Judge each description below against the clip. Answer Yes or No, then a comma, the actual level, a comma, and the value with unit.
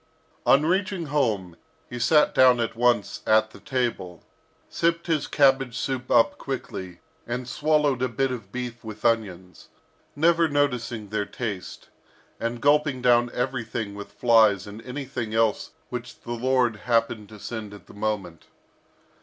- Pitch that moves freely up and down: No, average, 3.6 semitones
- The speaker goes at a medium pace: Yes, average, 145 wpm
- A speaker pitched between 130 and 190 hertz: No, low, 120 Hz